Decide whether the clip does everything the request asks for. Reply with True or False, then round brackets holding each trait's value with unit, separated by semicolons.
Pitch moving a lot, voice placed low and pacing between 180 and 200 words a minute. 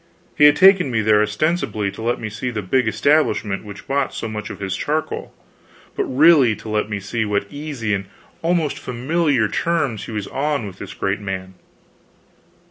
True (6.0 semitones; 115 Hz; 185 wpm)